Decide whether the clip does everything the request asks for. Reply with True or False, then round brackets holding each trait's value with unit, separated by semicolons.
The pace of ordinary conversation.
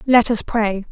True (195 wpm)